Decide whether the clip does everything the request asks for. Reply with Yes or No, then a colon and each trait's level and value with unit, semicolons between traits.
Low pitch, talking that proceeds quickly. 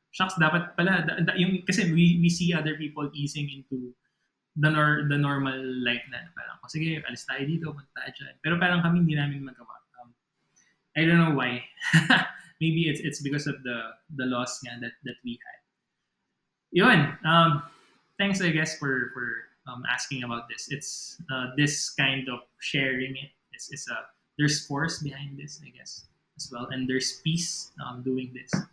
No: medium, 150 Hz; fast, 165 wpm